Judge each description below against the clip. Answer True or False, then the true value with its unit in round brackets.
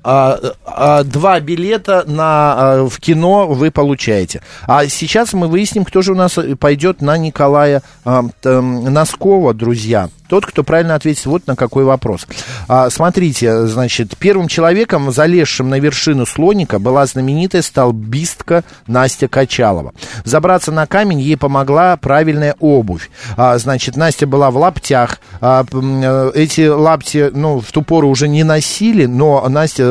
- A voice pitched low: False (145 Hz)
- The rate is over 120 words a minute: True (145 wpm)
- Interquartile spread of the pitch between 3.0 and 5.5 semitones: True (4.0 semitones)